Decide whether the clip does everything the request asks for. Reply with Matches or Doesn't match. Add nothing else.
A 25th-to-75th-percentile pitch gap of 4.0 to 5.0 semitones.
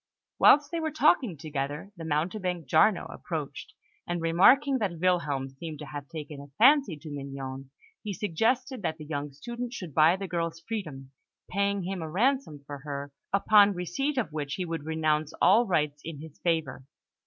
Doesn't match